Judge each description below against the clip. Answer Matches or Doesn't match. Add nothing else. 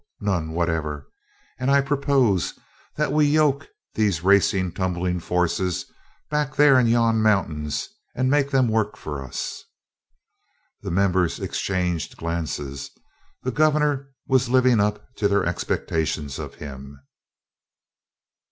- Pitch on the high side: Doesn't match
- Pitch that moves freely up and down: Matches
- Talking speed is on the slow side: Matches